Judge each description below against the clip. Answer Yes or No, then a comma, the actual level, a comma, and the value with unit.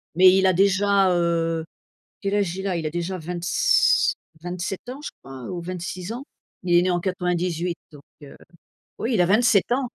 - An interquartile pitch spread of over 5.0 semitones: No, narrow, 2.6 semitones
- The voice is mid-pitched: Yes, medium, 180 Hz